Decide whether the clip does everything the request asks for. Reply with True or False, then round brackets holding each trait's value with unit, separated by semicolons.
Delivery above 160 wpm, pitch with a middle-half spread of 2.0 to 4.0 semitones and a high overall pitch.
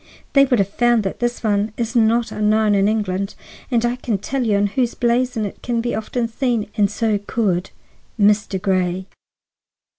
True (170 wpm; 2.8 semitones; 220 Hz)